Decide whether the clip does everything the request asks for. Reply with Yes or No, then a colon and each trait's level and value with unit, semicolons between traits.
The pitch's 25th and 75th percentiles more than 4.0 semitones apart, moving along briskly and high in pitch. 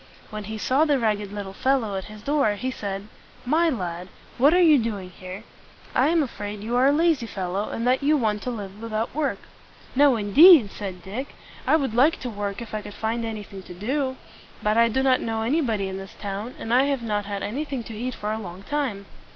Yes: average, 4.6 semitones; fast, 225 wpm; high, 225 Hz